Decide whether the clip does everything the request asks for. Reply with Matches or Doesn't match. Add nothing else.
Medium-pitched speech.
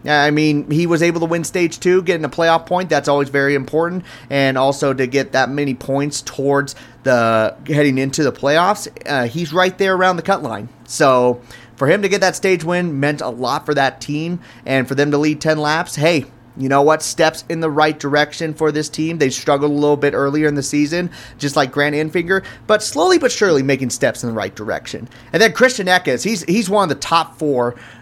Matches